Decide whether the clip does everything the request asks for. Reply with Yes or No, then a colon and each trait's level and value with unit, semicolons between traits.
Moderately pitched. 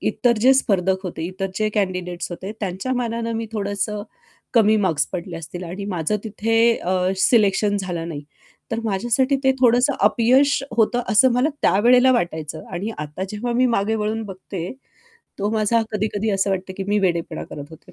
No: high, 205 Hz